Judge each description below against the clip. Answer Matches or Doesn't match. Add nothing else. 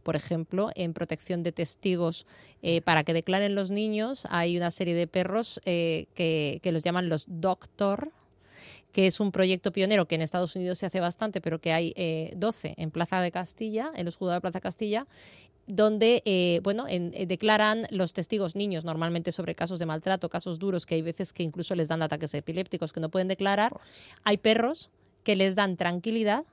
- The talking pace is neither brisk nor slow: Doesn't match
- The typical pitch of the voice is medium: Matches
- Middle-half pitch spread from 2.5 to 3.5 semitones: Matches